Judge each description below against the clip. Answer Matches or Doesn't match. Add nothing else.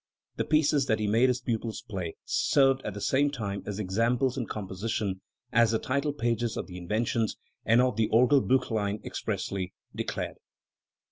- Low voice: Matches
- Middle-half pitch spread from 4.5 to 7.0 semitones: Doesn't match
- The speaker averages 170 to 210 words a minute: Doesn't match